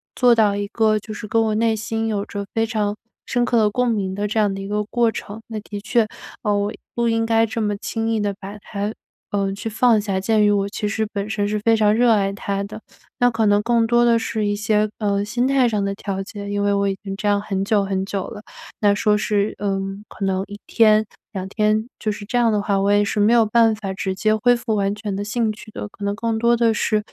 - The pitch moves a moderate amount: No, narrow, 1.8 semitones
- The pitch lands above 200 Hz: Yes, high, 210 Hz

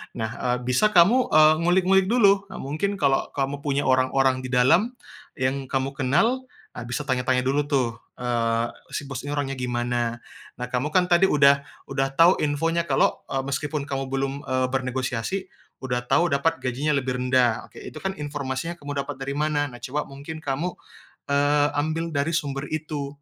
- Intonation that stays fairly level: No, average, 3.2 semitones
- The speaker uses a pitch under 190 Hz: Yes, medium, 140 Hz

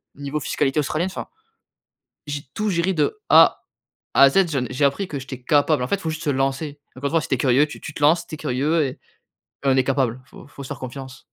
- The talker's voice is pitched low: No, medium, 145 Hz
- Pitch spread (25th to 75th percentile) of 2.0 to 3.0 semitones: Yes, narrow, 2.6 semitones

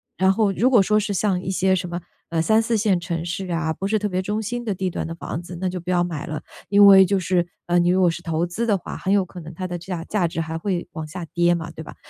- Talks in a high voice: No, medium, 180 Hz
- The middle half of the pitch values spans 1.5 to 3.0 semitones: Yes, narrow, 2.6 semitones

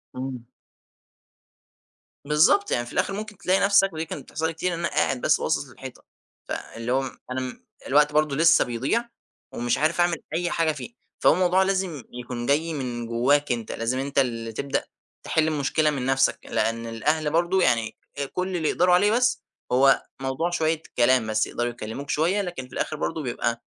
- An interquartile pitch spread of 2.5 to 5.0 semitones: No, wide, 5.6 semitones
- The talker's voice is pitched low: No, medium, 150 Hz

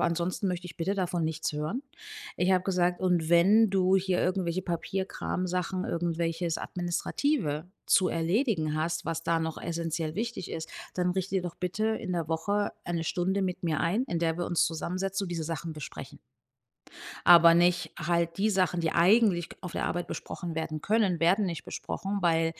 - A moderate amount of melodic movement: No, narrow, 2.3 semitones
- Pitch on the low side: No, medium, 175 Hz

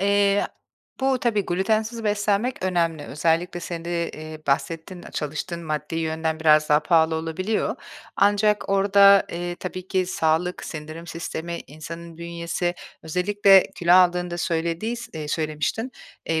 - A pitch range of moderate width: Yes, average, 3.6 semitones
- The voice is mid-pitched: Yes, medium, 175 Hz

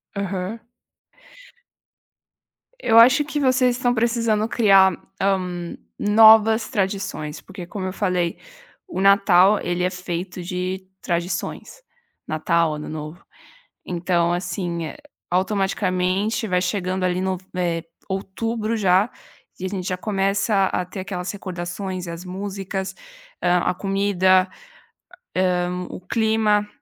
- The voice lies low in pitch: No, high, 190 Hz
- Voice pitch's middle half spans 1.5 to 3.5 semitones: Yes, narrow, 2.5 semitones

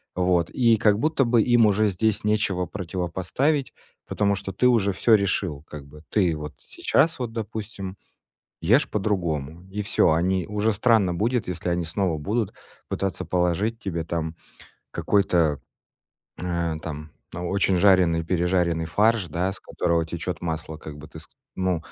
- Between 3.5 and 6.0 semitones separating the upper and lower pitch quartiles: Yes, average, 4.0 semitones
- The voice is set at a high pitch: No, very low, 95 Hz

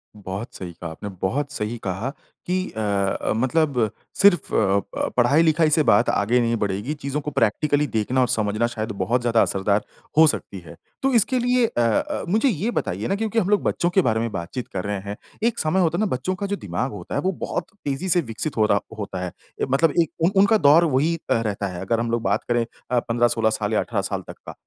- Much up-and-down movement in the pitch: Yes, wide, 7.7 semitones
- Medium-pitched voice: No, low, 120 Hz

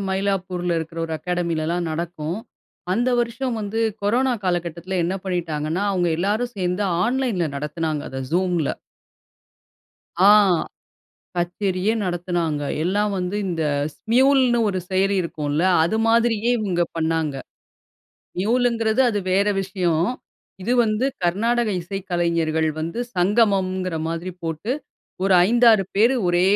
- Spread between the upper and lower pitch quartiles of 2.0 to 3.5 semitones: No, average, 4.1 semitones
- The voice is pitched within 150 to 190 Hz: Yes, medium, 185 Hz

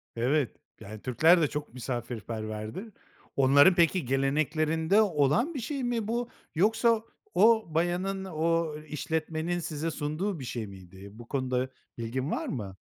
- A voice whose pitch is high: No, medium, 155 Hz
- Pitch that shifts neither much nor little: No, wide, 6.5 semitones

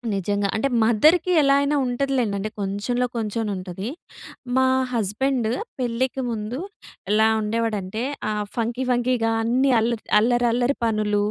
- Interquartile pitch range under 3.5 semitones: Yes, average, 2.9 semitones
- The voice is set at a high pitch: Yes, high, 230 Hz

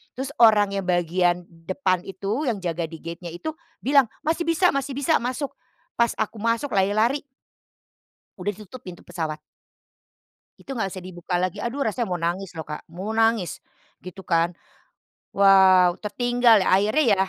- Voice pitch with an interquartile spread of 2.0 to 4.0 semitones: No, average, 5.2 semitones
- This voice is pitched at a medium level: No, high, 200 Hz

